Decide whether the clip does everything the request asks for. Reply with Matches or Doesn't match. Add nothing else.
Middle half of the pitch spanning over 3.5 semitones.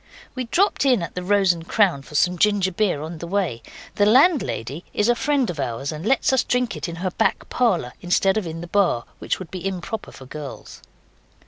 Matches